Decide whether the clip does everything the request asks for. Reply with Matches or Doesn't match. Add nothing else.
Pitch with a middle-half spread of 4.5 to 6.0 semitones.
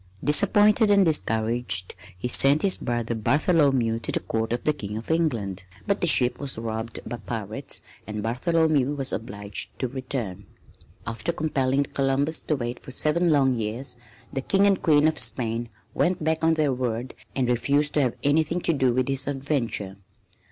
Matches